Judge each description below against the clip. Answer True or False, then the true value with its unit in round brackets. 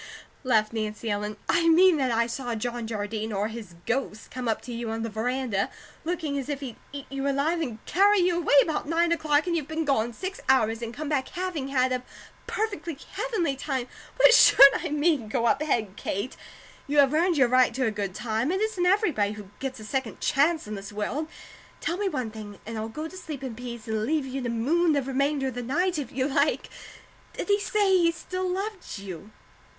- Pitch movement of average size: False (6.4 semitones)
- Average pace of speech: False (220 wpm)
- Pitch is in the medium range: False (270 Hz)